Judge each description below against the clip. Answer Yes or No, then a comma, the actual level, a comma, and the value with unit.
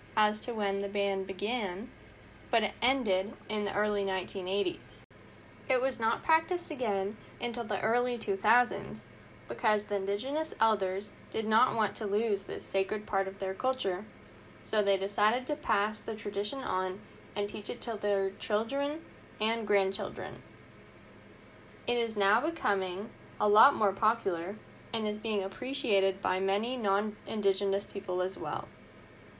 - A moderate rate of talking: Yes, average, 145 wpm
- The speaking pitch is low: No, high, 205 Hz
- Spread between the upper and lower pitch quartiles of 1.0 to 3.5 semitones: Yes, narrow, 2.5 semitones